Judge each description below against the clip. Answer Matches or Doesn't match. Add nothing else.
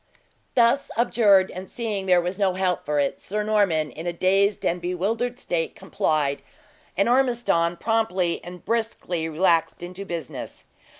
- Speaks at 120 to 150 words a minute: Matches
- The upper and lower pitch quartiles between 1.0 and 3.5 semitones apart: Doesn't match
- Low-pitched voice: Doesn't match